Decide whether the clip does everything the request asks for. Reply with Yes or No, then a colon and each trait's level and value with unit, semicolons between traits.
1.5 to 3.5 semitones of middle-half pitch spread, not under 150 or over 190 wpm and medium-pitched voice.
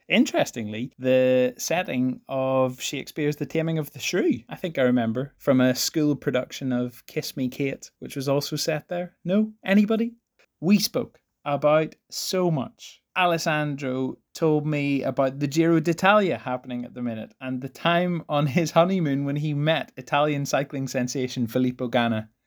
No: average, 4.4 semitones; average, 160 wpm; medium, 145 Hz